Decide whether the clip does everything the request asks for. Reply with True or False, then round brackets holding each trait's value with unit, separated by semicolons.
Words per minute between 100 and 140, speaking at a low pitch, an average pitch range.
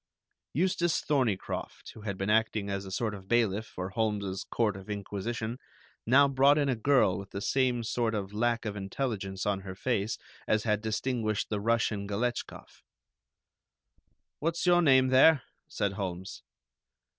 False (155 wpm; 110 Hz; 4.2 semitones)